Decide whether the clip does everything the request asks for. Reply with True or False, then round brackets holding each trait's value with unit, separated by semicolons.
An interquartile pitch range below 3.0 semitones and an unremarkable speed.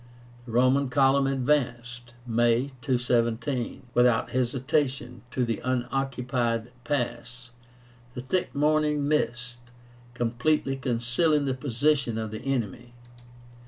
False (2.4 semitones; 100 wpm)